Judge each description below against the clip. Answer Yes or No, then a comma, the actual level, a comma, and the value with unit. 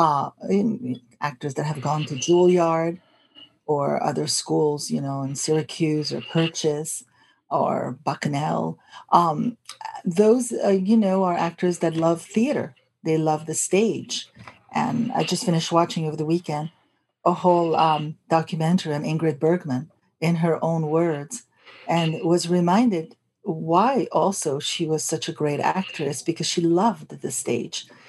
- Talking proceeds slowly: No, average, 145 wpm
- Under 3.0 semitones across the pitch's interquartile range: Yes, narrow, 2.6 semitones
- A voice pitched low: No, medium, 165 Hz